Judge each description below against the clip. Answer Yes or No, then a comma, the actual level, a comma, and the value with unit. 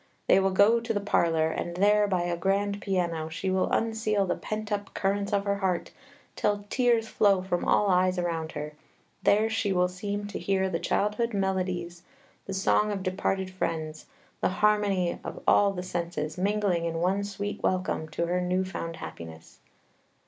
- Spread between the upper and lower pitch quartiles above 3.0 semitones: No, average, 2.7 semitones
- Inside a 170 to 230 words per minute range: Yes, average, 180 wpm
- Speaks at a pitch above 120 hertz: Yes, high, 190 Hz